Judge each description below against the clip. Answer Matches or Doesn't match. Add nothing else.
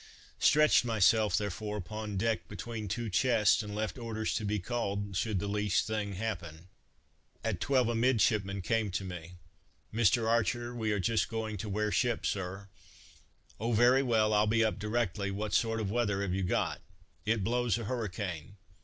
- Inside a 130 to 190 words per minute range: Matches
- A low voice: Matches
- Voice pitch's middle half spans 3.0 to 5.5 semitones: Doesn't match